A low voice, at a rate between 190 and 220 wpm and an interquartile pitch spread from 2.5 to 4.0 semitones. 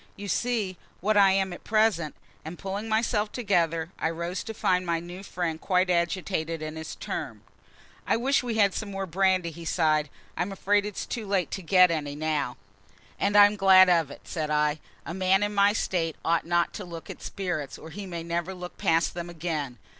No: medium, 180 Hz; average, 200 wpm; average, 3.4 semitones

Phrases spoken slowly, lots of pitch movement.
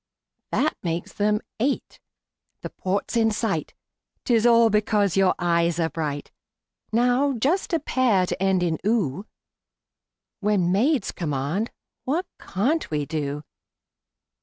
Yes: slow, 125 wpm; wide, 5.7 semitones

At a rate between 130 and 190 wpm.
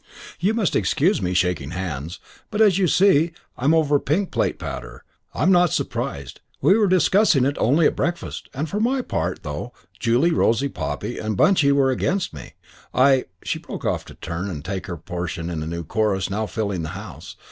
No: average, 200 wpm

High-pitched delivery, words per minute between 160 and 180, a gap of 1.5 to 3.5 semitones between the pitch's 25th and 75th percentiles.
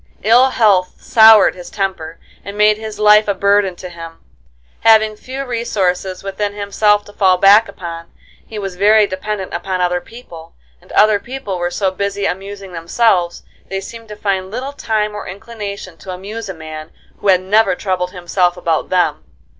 Yes: high, 200 Hz; average, 170 wpm; average, 2.8 semitones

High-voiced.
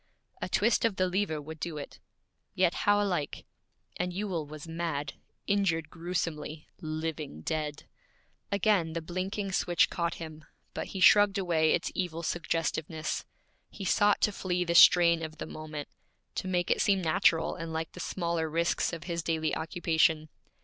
No: medium, 170 Hz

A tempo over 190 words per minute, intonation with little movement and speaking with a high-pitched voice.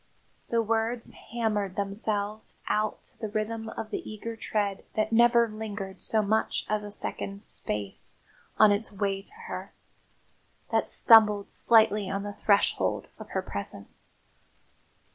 No: average, 140 wpm; narrow, 1.7 semitones; high, 215 Hz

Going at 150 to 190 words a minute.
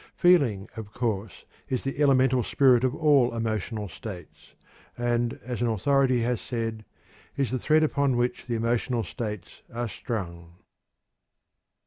No: slow, 135 wpm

